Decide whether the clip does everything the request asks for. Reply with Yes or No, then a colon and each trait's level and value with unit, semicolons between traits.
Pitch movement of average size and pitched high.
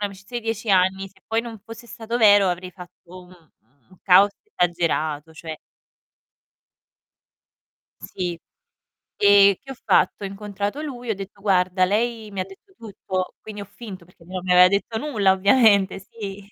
Yes: average, 3.0 semitones; high, 195 Hz